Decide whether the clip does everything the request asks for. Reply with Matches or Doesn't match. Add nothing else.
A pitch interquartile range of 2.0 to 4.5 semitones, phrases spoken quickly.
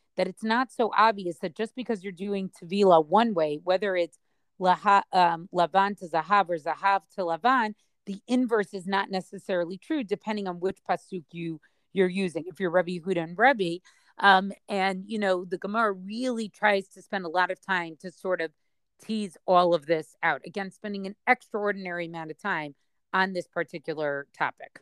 Doesn't match